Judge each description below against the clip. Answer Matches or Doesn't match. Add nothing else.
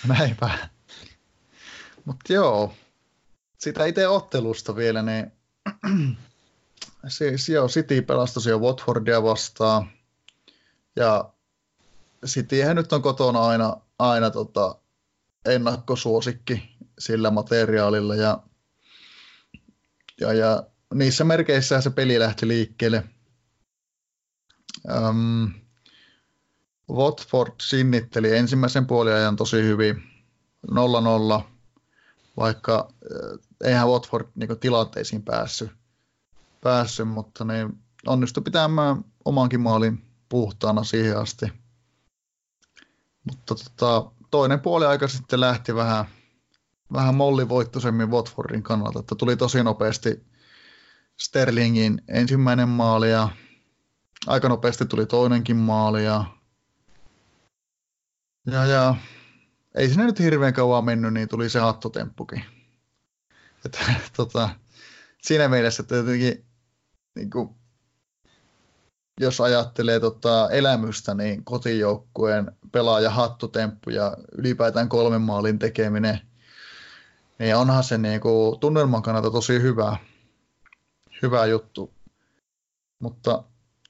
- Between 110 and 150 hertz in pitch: Matches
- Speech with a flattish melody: Matches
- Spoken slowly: Matches